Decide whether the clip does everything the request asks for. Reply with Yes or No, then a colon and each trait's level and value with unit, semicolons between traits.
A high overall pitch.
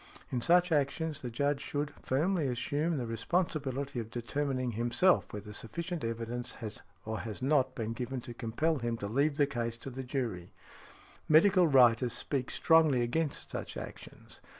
No: low, 130 Hz